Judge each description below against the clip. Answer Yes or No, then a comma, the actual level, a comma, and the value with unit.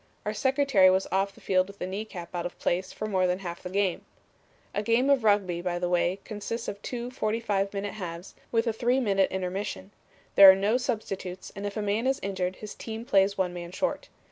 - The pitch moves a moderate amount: Yes, average, 3.0 semitones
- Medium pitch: No, high, 200 Hz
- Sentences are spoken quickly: Yes, fast, 220 wpm